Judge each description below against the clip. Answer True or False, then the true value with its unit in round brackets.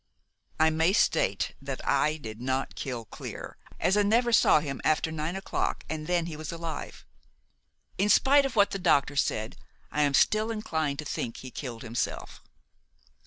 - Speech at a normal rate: True (170 wpm)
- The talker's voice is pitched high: False (155 Hz)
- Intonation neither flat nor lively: False (6.0 semitones)